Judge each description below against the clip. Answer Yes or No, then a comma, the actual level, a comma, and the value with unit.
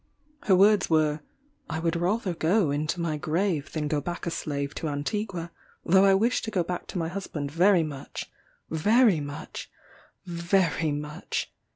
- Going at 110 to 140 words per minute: No, average, 165 wpm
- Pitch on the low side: No, medium, 170 Hz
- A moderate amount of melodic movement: Yes, average, 4.1 semitones